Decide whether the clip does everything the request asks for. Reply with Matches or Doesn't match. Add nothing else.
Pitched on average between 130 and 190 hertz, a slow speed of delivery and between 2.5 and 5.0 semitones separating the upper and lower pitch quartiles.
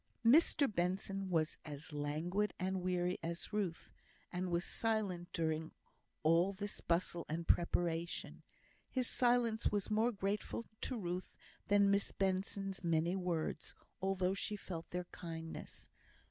Matches